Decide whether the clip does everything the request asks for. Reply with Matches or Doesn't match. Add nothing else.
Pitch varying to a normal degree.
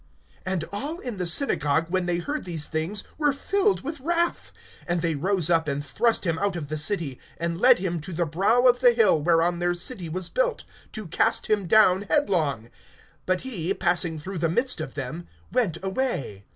Doesn't match